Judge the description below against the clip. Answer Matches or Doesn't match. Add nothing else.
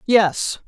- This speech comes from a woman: Matches